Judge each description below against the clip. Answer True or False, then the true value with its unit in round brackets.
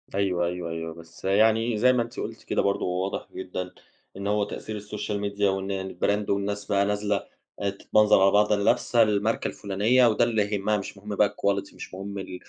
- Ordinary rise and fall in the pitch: False (1.5 semitones)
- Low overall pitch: True (100 Hz)